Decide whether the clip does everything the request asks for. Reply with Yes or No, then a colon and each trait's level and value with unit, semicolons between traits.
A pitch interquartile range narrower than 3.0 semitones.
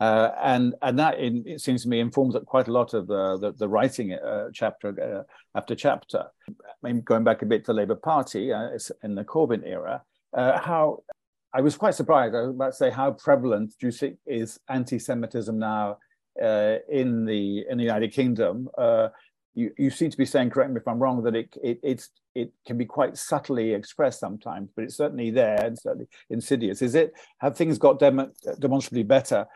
No: average, 3.3 semitones